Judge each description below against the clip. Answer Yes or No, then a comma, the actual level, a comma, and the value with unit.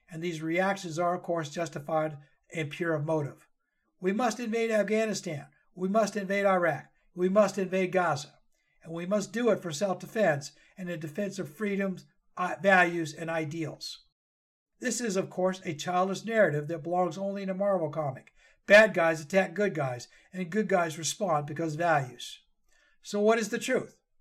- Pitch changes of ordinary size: Yes, average, 3.6 semitones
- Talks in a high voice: No, medium, 180 Hz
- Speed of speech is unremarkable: Yes, average, 170 wpm